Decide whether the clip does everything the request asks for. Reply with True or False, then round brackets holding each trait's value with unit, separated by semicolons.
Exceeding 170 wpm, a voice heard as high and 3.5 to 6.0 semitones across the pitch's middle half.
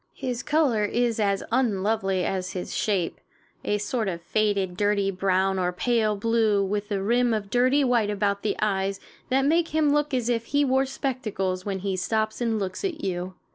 True (185 wpm; 210 Hz; 4.1 semitones)